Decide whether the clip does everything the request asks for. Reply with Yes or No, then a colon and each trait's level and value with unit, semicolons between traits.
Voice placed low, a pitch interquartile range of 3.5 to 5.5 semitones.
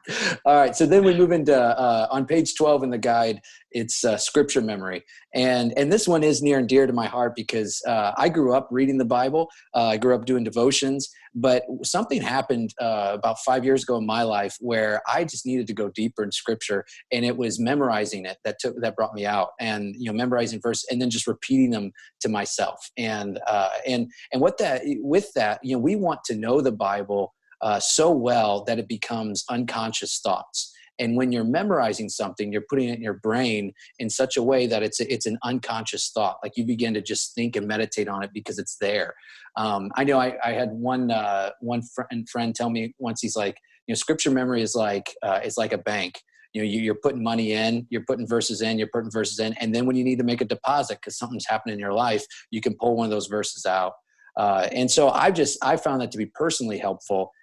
No: low, 115 Hz; average, 2.8 semitones